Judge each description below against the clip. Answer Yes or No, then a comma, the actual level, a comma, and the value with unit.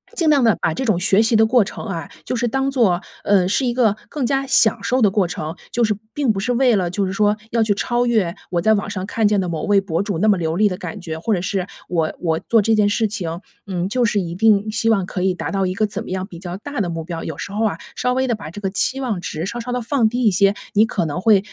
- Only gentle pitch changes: No, average, 3.9 semitones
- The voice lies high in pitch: Yes, high, 205 Hz